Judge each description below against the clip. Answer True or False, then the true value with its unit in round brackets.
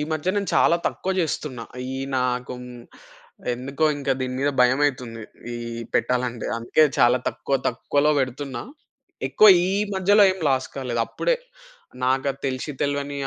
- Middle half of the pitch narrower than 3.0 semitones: True (2.6 semitones)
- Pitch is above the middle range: False (135 Hz)